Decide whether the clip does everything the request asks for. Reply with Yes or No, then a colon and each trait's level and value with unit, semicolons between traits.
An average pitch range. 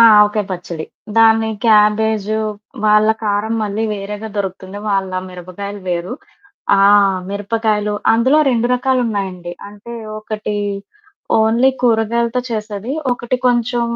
No: narrow, 2.1 semitones